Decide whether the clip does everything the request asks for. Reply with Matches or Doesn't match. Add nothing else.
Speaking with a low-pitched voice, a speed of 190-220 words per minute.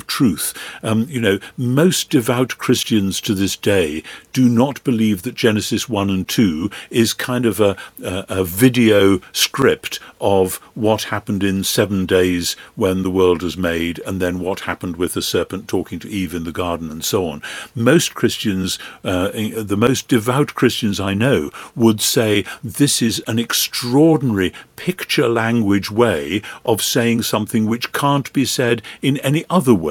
Doesn't match